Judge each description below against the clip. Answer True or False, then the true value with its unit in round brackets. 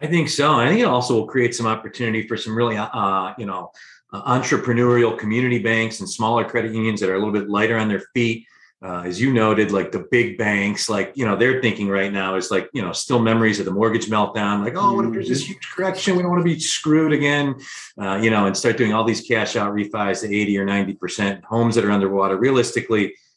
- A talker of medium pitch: False (115 Hz)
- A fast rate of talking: True (240 wpm)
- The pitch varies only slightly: False (3.0 semitones)